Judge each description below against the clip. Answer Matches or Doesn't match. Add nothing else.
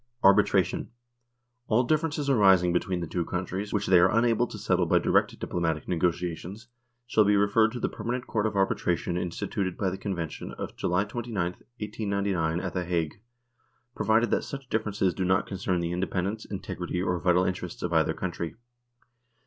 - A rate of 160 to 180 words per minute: Matches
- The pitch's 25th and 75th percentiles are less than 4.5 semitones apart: Matches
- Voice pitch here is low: Matches